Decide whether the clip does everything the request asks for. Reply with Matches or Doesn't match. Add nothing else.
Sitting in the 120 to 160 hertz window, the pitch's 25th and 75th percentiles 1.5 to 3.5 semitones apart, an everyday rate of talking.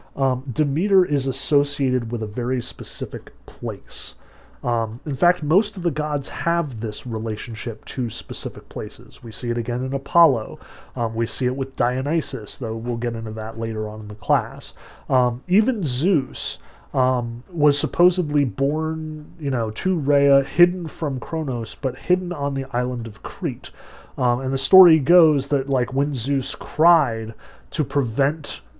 Doesn't match